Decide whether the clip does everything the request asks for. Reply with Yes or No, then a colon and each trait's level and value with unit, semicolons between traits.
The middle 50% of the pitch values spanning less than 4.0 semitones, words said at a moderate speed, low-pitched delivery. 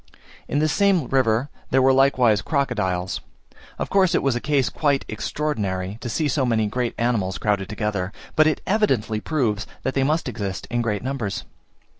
No: average, 5.2 semitones; average, 175 wpm; low, 125 Hz